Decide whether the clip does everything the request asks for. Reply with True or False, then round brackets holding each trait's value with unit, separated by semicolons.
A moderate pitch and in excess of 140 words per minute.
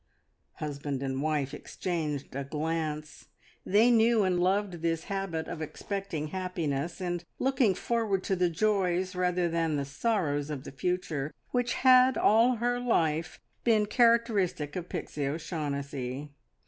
False (175 Hz; 135 wpm)